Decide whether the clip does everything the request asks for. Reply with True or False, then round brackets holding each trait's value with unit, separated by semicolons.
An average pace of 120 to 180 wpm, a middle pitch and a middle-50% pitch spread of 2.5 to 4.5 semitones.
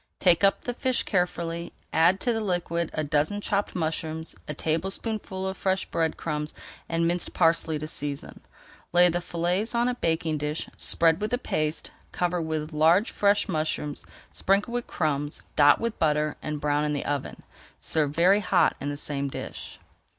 True (170 wpm; 165 Hz; 3.9 semitones)